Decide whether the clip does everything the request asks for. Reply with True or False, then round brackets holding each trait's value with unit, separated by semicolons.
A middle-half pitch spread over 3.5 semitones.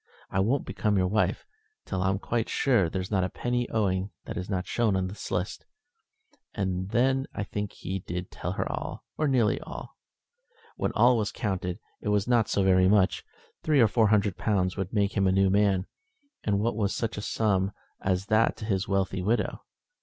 False (2.7 semitones)